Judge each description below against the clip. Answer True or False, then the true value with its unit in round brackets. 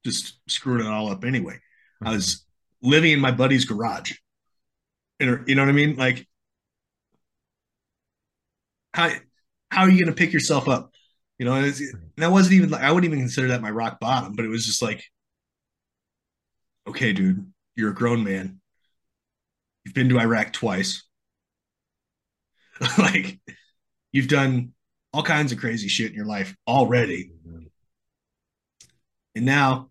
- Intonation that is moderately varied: True (5.0 semitones)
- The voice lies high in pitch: False (125 Hz)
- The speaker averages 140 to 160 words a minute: True (155 wpm)